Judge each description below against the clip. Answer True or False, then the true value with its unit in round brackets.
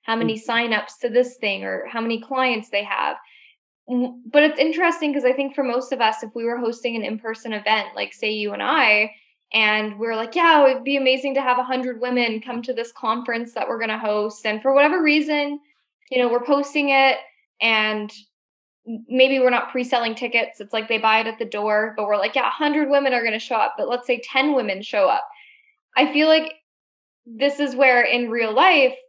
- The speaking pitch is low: False (245 Hz)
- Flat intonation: False (3.8 semitones)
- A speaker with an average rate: False (220 wpm)